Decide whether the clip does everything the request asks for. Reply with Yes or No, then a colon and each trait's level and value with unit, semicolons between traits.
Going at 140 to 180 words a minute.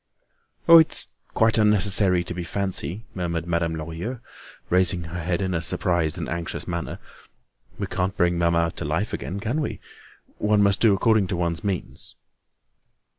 Yes: average, 160 wpm